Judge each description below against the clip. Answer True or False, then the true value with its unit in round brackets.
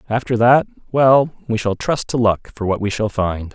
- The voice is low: True (115 Hz)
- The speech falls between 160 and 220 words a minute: True (205 wpm)